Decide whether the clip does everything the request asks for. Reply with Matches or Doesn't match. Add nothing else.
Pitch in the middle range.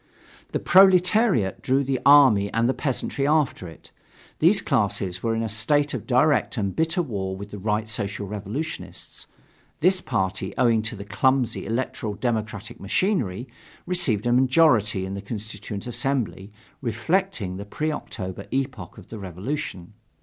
Doesn't match